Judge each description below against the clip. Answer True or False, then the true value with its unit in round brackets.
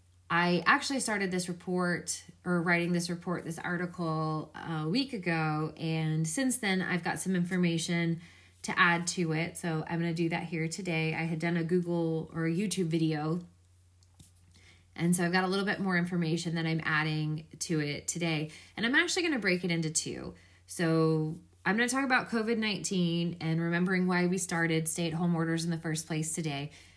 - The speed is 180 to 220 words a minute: True (195 wpm)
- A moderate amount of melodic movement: False (2.2 semitones)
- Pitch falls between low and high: True (170 Hz)